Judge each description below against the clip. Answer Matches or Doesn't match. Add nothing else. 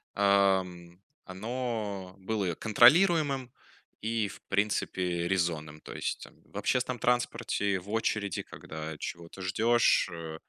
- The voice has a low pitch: Matches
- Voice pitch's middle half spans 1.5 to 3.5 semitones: Doesn't match